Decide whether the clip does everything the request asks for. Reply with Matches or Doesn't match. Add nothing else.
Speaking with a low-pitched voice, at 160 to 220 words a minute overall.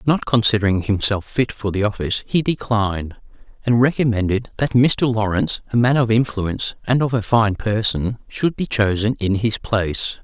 Matches